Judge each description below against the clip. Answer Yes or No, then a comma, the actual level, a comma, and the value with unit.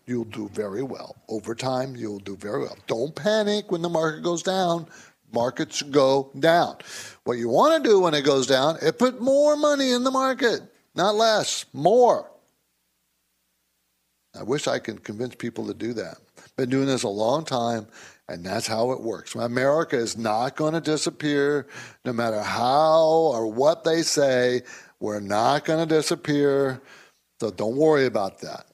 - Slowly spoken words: No, average, 170 wpm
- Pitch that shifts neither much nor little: No, wide, 6.4 semitones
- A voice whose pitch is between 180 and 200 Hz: No, low, 135 Hz